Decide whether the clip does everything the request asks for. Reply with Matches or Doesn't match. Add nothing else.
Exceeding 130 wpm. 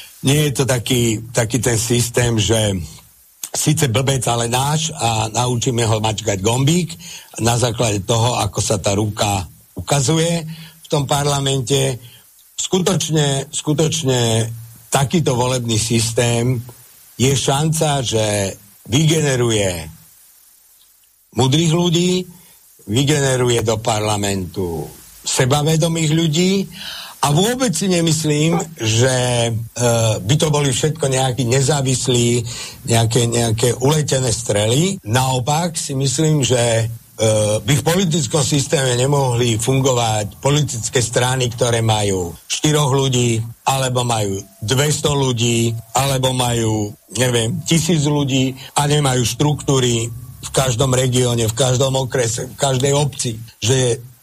Doesn't match